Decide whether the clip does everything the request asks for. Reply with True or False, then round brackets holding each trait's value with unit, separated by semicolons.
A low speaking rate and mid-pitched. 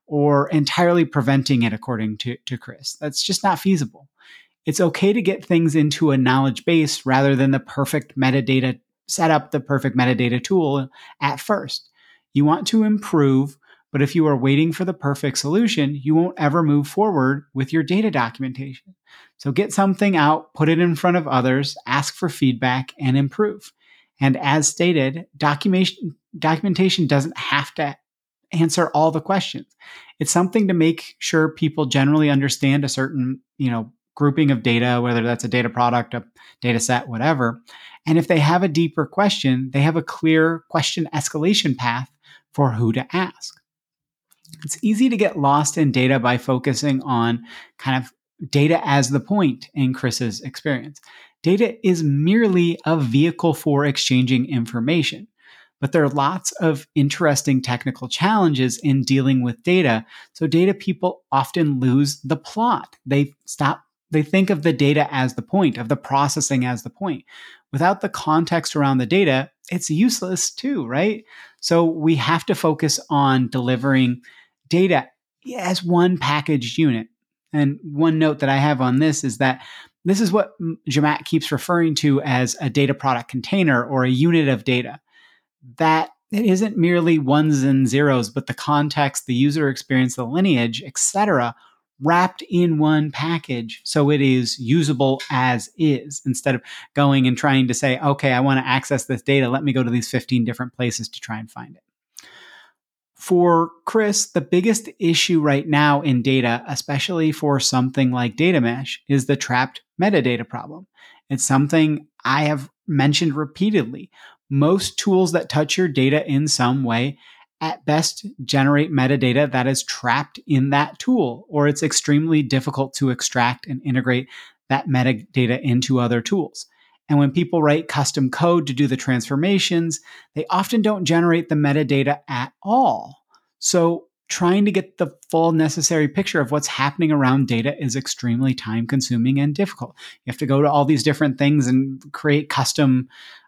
False (165 wpm; 145 Hz)